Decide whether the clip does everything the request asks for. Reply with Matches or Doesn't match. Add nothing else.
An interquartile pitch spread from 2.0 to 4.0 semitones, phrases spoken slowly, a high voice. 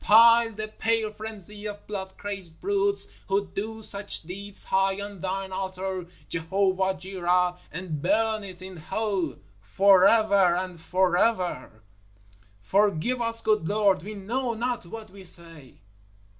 Matches